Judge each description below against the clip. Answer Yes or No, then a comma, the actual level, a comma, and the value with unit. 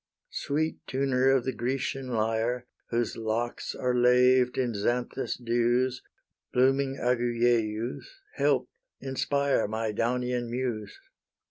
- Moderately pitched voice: No, low, 125 Hz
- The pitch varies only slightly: Yes, narrow, 1.8 semitones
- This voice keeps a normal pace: No, slow, 105 wpm